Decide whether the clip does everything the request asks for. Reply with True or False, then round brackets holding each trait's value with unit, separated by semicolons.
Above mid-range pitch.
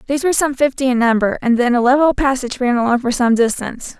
True (255 Hz)